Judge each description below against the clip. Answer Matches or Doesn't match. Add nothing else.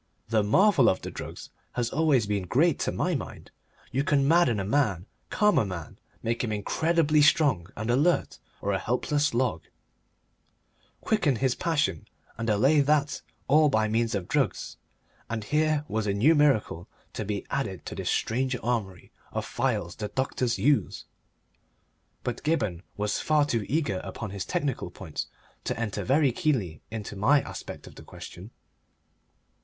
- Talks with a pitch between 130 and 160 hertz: Doesn't match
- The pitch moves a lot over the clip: Matches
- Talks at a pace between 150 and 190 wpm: Matches